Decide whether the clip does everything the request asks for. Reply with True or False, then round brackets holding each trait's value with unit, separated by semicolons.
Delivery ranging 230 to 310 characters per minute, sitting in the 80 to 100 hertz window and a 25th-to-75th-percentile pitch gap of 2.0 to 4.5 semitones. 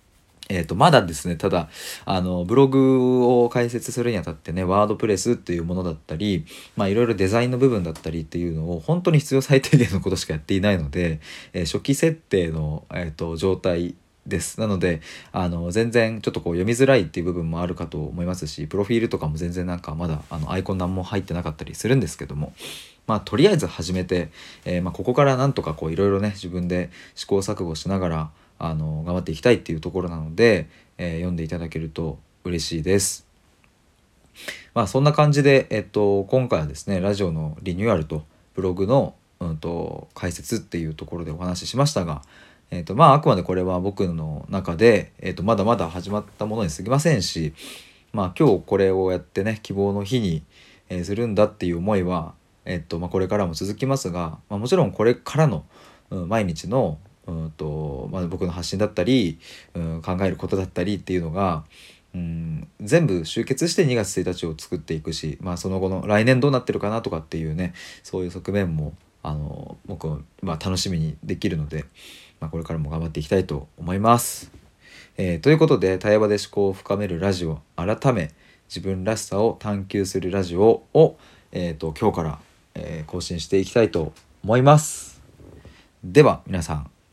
False (395 characters per minute; 90 Hz; 4.1 semitones)